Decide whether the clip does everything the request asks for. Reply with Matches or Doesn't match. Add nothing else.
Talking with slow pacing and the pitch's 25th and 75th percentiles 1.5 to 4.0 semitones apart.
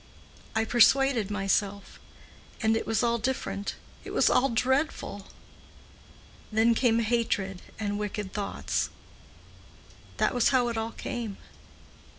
Matches